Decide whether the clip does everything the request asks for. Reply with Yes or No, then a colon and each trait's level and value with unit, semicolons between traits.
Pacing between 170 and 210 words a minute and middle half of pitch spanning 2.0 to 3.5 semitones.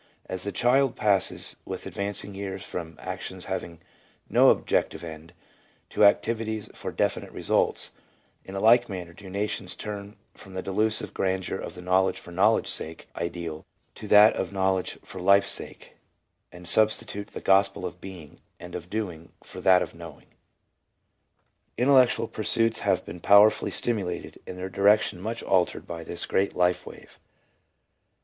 No: average, 155 wpm; average, 2.9 semitones